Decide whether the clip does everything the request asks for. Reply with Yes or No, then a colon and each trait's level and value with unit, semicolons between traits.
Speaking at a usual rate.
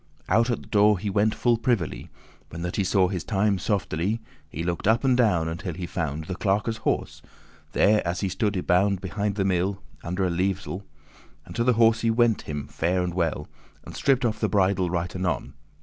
No: fast, 210 wpm